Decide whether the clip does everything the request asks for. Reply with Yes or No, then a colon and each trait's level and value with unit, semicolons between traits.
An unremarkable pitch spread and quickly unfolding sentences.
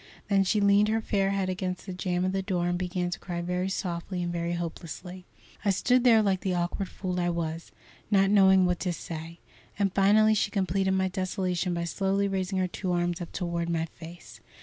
No: narrow, 1.9 semitones; fast, 210 wpm